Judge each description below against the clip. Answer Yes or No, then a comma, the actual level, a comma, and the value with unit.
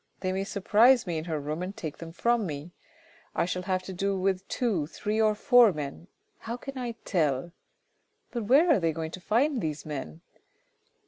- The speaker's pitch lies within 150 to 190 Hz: Yes, medium, 185 Hz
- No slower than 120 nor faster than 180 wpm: No, average, 195 wpm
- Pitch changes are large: Yes, wide, 5.9 semitones